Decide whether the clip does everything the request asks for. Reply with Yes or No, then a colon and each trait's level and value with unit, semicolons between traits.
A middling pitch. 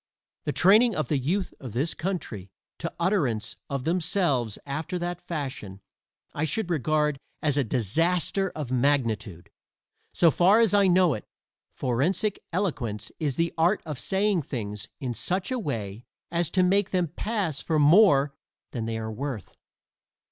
Yes: medium, 155 Hz